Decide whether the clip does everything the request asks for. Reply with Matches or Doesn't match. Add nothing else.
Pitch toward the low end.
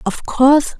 Doesn't match